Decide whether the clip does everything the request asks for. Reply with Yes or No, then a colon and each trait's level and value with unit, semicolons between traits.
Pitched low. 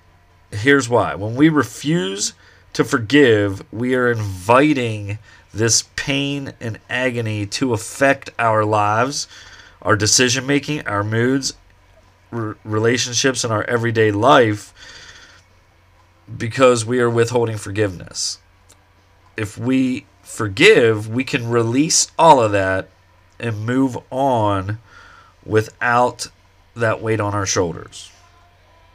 Yes: low, 110 Hz